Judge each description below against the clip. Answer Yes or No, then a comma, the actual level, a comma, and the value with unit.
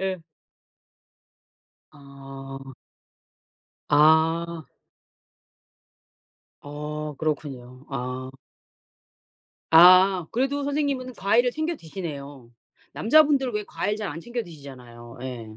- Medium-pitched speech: Yes, medium, 160 Hz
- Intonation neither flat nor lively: No, wide, 7.5 semitones